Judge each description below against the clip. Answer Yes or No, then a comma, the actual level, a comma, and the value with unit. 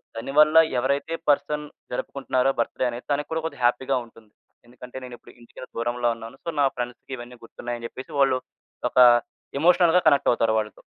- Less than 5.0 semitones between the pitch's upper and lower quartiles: Yes, average, 2.9 semitones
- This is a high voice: No, low, 125 Hz